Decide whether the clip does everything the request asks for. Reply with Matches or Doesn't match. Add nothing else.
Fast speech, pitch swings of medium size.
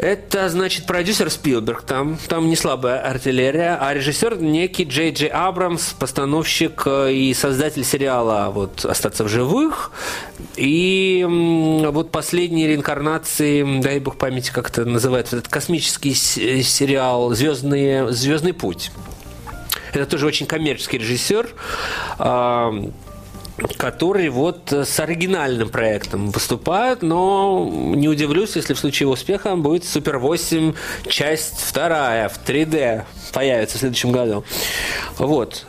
Doesn't match